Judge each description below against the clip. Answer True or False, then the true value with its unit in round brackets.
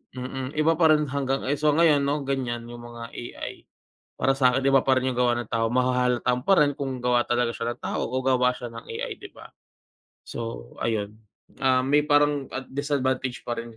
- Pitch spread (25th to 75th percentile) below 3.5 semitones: True (2.7 semitones)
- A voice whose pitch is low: True (130 Hz)